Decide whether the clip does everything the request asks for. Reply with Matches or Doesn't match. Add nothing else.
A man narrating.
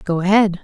Doesn't match